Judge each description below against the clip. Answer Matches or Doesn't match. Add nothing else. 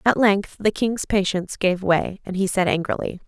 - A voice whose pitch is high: Matches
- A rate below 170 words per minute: Doesn't match